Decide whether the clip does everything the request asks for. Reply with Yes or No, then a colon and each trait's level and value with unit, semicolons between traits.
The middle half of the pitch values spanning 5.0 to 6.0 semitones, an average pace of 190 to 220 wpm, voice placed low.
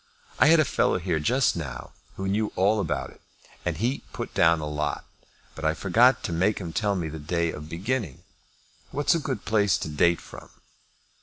Yes: wide, 5.6 semitones; average, 200 wpm; very low, 90 Hz